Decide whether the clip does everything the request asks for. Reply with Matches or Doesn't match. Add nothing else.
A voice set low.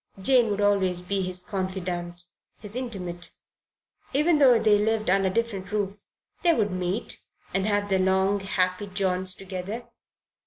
Doesn't match